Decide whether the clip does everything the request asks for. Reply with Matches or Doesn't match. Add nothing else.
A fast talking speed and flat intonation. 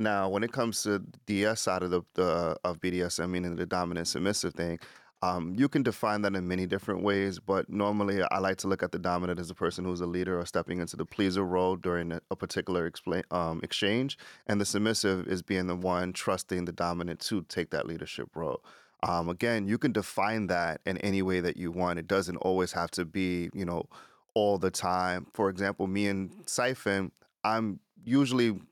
Matches